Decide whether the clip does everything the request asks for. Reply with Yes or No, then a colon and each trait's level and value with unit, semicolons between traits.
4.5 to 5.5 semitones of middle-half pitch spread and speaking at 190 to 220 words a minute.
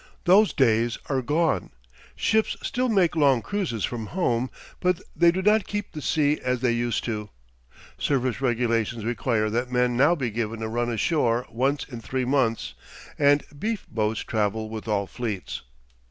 No: average, 4.8 semitones; average, 165 wpm